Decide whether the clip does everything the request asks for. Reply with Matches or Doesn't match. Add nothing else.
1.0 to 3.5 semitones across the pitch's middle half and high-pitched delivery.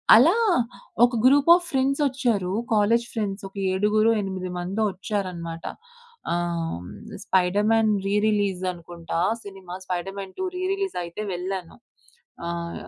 Doesn't match